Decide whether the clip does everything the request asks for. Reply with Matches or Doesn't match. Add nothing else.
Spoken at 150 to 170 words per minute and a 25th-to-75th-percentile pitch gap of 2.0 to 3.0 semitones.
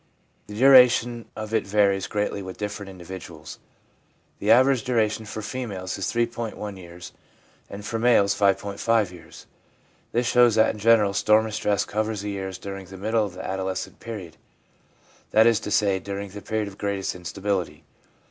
Matches